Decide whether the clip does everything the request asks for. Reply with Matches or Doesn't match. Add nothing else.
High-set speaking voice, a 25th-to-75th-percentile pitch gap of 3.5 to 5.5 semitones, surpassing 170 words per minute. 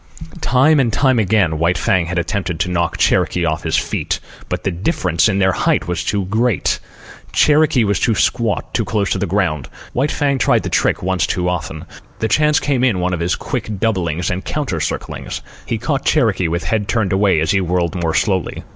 Doesn't match